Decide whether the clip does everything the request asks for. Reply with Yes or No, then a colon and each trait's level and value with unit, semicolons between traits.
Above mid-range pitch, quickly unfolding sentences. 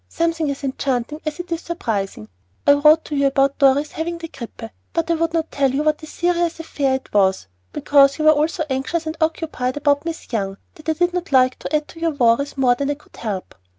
Yes: very high, 290 Hz; fast, 230 wpm